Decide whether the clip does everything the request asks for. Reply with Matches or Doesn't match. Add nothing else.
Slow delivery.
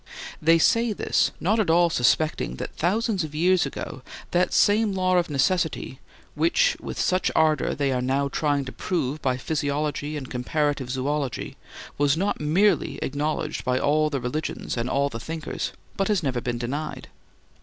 Doesn't match